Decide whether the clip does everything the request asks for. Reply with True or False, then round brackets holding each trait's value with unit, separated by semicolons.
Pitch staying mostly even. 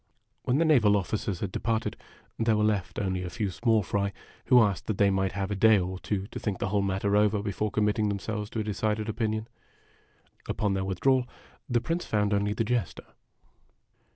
True (2.0 semitones)